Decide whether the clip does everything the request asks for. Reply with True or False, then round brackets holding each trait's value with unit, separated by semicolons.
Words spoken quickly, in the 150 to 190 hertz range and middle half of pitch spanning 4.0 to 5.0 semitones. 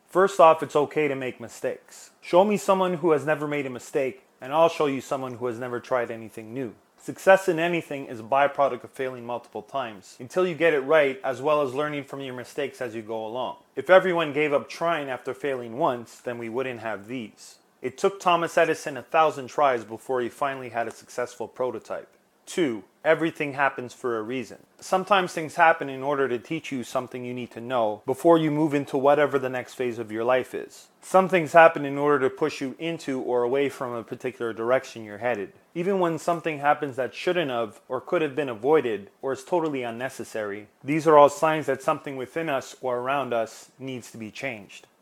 False (210 wpm; 135 Hz; 4.3 semitones)